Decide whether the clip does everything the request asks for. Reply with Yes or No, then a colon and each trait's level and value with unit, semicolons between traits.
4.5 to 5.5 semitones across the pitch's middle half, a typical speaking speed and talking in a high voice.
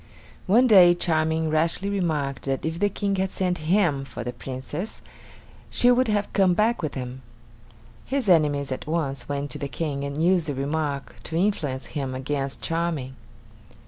No: average, 5.1 semitones; average, 170 wpm; medium, 160 Hz